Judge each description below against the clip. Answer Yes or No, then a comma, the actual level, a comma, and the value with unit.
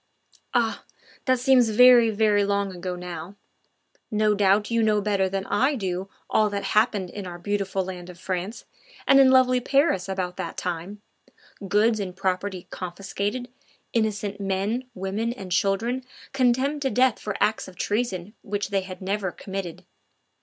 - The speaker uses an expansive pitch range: No, average, 3.4 semitones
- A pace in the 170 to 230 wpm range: No, average, 155 wpm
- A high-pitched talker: Yes, high, 205 Hz